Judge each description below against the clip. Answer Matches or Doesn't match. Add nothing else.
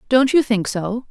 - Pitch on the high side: Matches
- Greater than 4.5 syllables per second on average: Doesn't match